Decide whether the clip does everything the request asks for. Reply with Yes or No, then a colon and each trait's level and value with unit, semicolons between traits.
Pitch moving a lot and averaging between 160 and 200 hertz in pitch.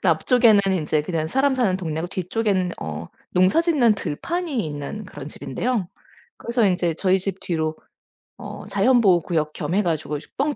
Yes: wide, 6.6 semitones; medium, 185 Hz